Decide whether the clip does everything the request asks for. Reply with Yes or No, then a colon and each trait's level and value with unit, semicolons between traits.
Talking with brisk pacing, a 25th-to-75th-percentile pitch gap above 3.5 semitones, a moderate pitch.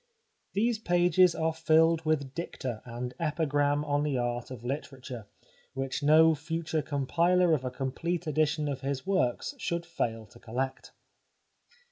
No: average, 140 wpm; average, 4.1 semitones; medium, 150 Hz